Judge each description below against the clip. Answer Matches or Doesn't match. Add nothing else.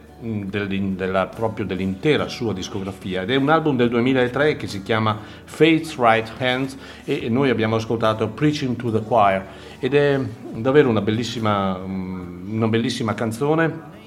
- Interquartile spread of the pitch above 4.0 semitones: Matches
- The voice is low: Matches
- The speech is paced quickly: Doesn't match